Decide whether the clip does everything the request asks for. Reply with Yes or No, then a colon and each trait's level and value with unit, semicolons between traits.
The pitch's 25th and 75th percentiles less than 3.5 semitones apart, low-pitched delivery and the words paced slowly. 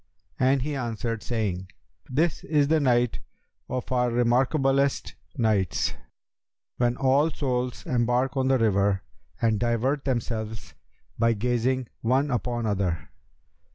Yes: average, 2.8 semitones; low, 125 Hz; slow, 120 wpm